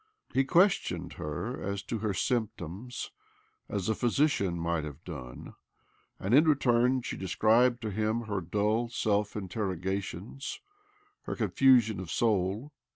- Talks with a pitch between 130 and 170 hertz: No, low, 105 Hz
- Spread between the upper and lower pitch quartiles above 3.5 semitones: Yes, average, 4.4 semitones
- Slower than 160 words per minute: Yes, average, 140 wpm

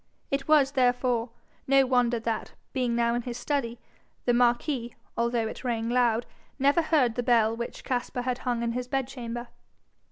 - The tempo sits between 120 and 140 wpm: No, average, 165 wpm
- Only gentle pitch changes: Yes, narrow, 1.8 semitones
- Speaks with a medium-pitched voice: No, high, 245 Hz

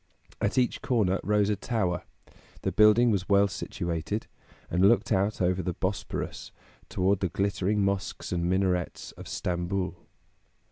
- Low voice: Yes, very low, 95 Hz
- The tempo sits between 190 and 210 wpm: No, average, 140 wpm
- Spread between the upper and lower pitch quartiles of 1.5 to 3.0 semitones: Yes, narrow, 2.5 semitones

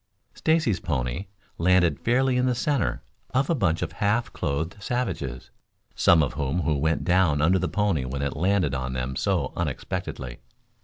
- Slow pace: No, average, 160 wpm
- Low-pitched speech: Yes, very low, 85 Hz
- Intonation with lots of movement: Yes, wide, 7.1 semitones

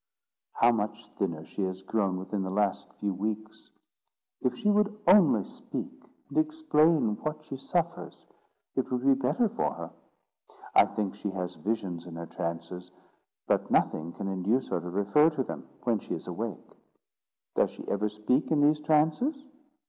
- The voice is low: Yes, low, 110 Hz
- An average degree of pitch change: No, wide, 8.2 semitones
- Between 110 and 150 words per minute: No, average, 165 wpm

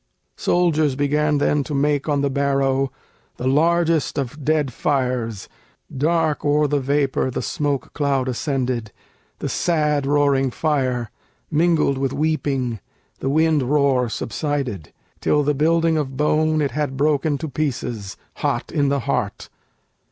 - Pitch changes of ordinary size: No, narrow, 2.3 semitones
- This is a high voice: No, medium, 145 Hz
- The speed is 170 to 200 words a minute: No, slow, 135 wpm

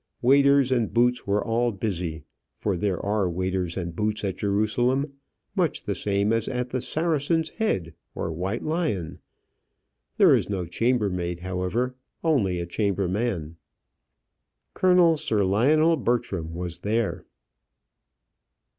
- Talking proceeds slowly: Yes, slow, 125 wpm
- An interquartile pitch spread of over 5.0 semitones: Yes, wide, 5.5 semitones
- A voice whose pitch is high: No, low, 105 Hz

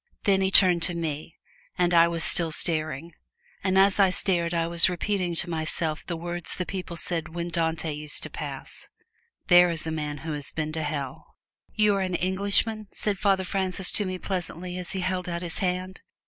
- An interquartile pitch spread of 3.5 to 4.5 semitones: No, narrow, 2.4 semitones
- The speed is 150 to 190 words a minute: No, average, 200 wpm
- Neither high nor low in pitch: Yes, medium, 175 Hz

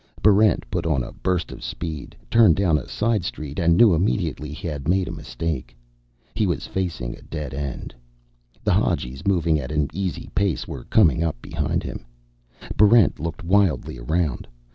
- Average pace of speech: Yes, average, 170 wpm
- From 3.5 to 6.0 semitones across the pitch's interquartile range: Yes, average, 4.2 semitones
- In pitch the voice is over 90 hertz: No, very low, 85 Hz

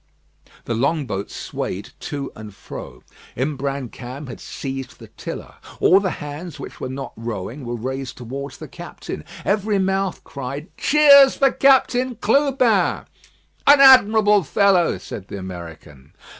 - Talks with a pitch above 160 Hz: No, medium, 140 Hz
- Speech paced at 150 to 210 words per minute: No, slow, 135 wpm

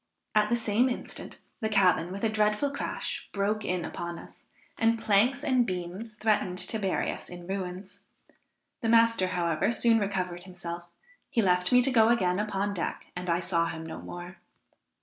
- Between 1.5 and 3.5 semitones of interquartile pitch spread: No, average, 3.9 semitones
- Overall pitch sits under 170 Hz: No, high, 200 Hz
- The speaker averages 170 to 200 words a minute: Yes, average, 175 wpm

